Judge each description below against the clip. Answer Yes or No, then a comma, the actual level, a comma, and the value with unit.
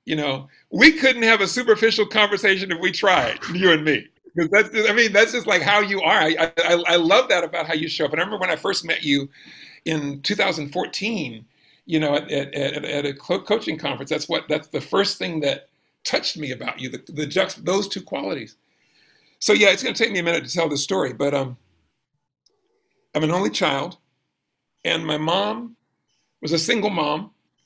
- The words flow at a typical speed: No, fast, 210 wpm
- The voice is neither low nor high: Yes, medium, 175 Hz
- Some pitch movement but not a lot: No, wide, 6.2 semitones